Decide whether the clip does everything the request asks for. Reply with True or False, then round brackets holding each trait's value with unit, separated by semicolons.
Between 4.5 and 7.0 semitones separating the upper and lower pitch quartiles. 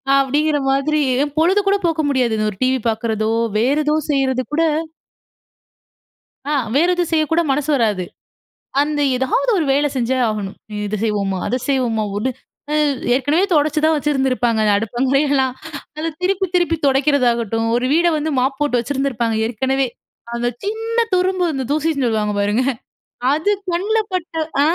True (4.8 semitones)